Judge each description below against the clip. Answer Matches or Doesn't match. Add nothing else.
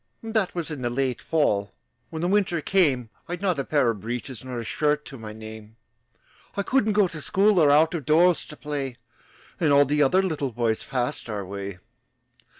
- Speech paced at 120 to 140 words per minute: Doesn't match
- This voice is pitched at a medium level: Matches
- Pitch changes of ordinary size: Doesn't match